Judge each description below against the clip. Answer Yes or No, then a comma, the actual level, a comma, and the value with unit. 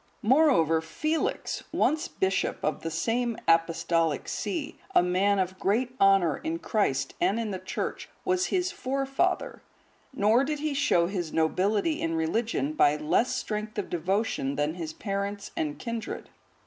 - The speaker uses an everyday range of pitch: No, wide, 7.5 semitones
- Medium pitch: No, high, 200 Hz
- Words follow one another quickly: No, average, 150 wpm